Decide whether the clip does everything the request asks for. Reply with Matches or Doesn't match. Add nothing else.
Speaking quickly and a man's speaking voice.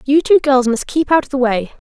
Doesn't match